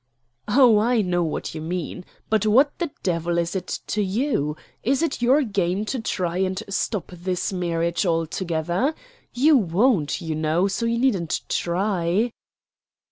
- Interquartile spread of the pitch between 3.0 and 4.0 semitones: No, average, 5.3 semitones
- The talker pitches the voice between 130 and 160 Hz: No, high, 190 Hz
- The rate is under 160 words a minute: Yes, average, 150 wpm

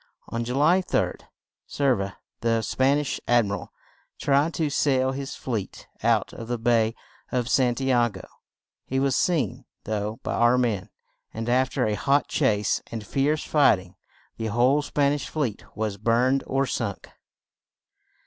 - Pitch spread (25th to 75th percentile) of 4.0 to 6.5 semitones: No, average, 3.6 semitones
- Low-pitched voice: Yes, low, 125 Hz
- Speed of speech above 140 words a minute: Yes, average, 175 wpm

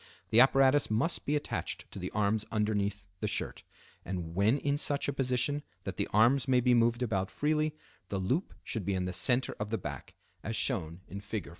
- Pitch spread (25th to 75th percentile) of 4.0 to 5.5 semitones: Yes, average, 5.2 semitones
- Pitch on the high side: No, low, 110 Hz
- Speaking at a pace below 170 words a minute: No, average, 200 wpm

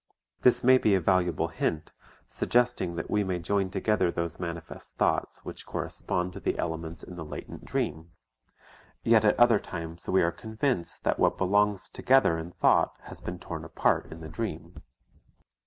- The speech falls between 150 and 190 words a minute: Yes, average, 170 wpm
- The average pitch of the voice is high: No, very low, 90 Hz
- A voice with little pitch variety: No, average, 4.0 semitones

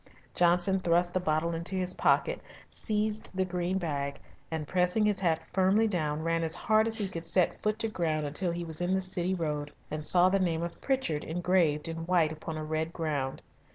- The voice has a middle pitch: Yes, medium, 175 Hz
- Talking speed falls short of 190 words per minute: No, fast, 205 wpm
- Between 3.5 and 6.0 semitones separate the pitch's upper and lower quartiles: No, average, 2.9 semitones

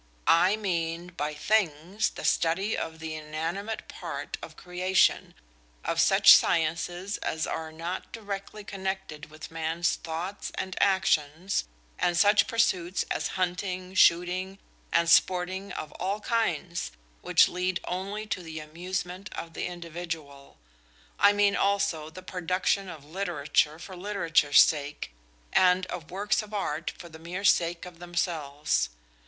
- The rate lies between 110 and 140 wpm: Yes, slow, 135 wpm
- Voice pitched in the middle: Yes, medium, 180 Hz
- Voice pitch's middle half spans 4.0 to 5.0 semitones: No, average, 2.9 semitones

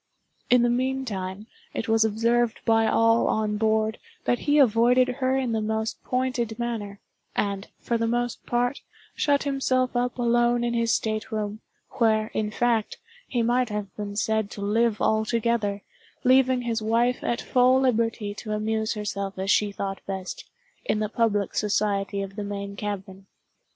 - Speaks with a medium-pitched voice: No, high, 225 Hz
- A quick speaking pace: No, average, 160 wpm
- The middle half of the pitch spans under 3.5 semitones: Yes, narrow, 2.6 semitones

